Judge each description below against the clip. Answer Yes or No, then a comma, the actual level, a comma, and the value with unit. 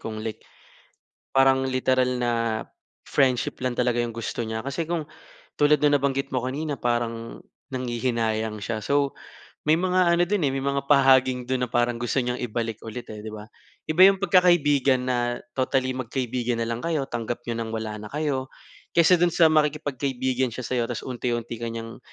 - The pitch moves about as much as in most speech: Yes, average, 3.1 semitones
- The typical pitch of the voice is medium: No, low, 130 Hz